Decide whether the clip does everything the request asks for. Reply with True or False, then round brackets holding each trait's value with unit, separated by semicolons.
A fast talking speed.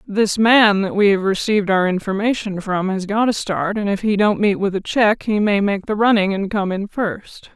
True (240 wpm)